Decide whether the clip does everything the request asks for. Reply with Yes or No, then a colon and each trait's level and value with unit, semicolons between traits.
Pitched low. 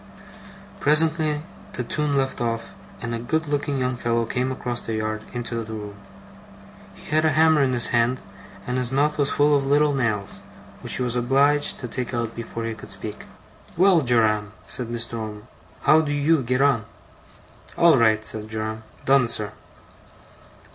Yes: low, 125 Hz